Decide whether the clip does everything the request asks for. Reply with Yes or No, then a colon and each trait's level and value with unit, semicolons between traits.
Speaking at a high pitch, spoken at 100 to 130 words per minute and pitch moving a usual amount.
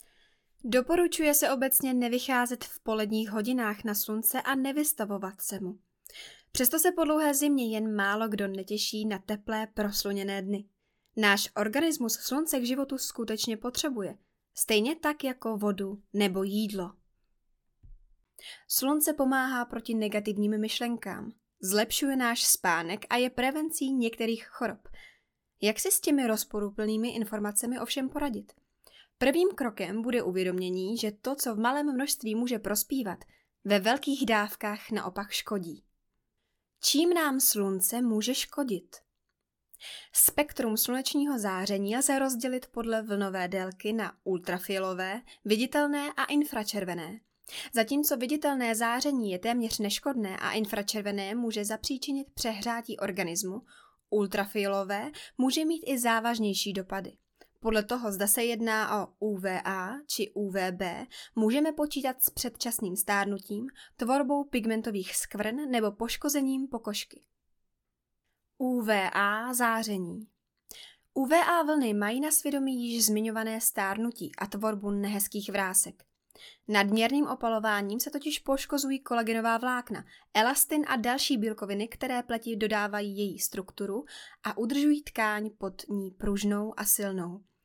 Yes: high, 225 Hz; slow, 115 wpm; average, 4.3 semitones